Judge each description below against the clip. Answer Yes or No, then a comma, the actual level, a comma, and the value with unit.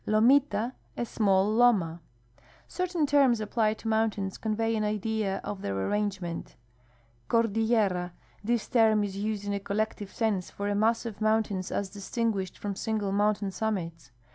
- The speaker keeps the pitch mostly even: Yes, narrow, 2.2 semitones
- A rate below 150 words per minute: No, average, 160 wpm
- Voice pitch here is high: Yes, high, 210 Hz